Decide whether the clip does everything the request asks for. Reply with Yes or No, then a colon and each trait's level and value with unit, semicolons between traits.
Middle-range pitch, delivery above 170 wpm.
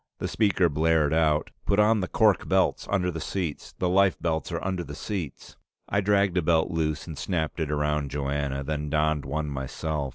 No: very low, 80 Hz; average, 190 wpm